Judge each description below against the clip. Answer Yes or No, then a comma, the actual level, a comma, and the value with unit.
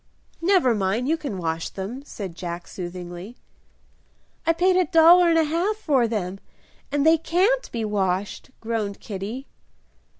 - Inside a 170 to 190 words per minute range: No, average, 145 wpm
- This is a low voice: No, high, 235 Hz